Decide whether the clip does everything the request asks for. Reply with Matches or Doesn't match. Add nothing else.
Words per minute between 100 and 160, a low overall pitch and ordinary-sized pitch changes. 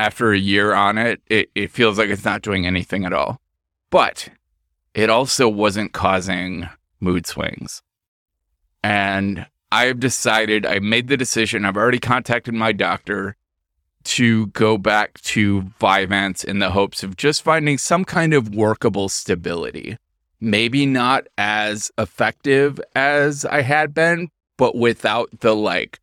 Matches